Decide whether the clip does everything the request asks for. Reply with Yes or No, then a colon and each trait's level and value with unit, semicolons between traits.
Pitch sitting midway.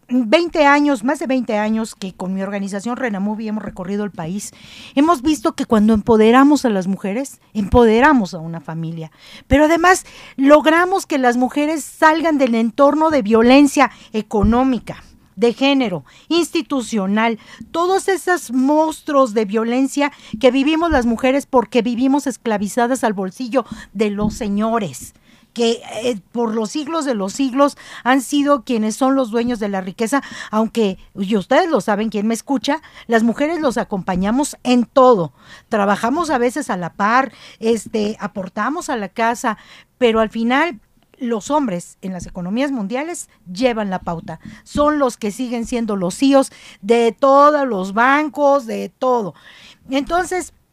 No: high, 240 Hz